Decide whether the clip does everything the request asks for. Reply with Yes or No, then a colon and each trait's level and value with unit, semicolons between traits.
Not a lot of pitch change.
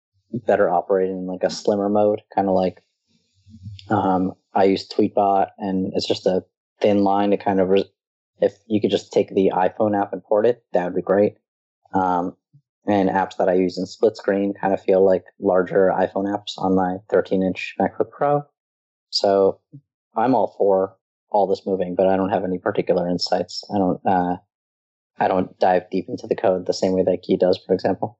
Yes: narrow, 1.4 semitones